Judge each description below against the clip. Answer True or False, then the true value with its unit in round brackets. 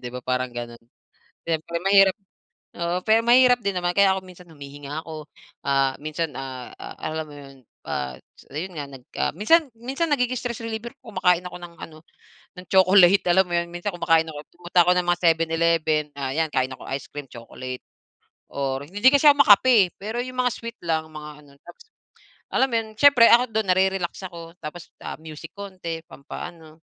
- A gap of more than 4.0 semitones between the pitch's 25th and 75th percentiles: True (4.9 semitones)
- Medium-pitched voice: True (170 Hz)